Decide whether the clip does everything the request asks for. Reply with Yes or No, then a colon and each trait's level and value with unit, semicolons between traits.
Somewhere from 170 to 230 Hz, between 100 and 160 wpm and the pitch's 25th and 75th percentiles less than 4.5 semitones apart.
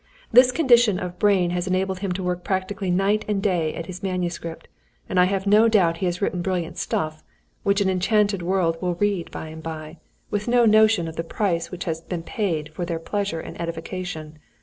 No: medium, 185 Hz; fast, 205 wpm; average, 3.2 semitones